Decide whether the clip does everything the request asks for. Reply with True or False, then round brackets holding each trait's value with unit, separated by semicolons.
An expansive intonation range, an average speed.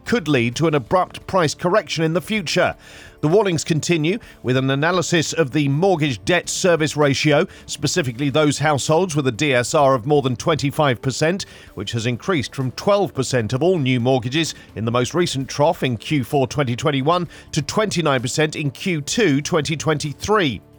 False (4.3 semitones; 155 wpm)